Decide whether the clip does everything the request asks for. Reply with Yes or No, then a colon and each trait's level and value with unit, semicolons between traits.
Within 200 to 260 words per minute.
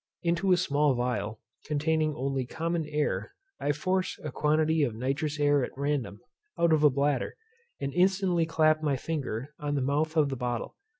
No: average, 175 wpm